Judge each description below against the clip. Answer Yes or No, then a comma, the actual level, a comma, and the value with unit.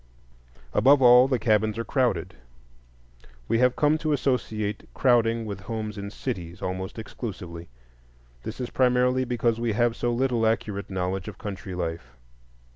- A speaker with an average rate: Yes, average, 145 wpm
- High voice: No, low, 115 Hz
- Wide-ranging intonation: No, average, 4.1 semitones